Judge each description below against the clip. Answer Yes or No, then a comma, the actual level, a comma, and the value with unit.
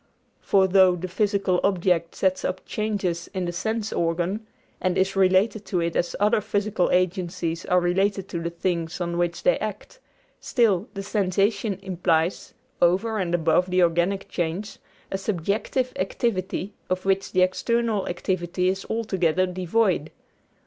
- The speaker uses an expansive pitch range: No, narrow, 2.5 semitones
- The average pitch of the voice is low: No, medium, 185 Hz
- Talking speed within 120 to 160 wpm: Yes, average, 150 wpm